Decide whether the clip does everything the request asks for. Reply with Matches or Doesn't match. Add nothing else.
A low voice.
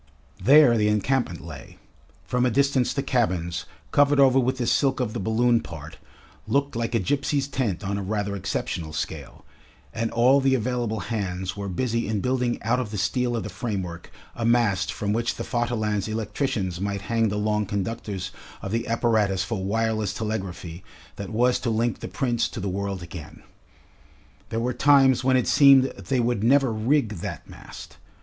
Matches